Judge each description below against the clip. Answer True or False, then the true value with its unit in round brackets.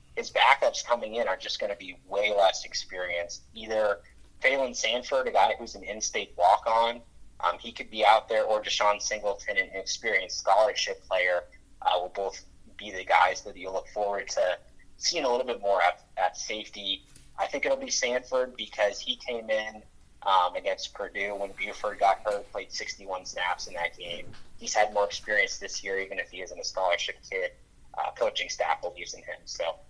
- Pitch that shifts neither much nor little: False (8.1 semitones)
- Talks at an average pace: True (190 wpm)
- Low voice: True (105 Hz)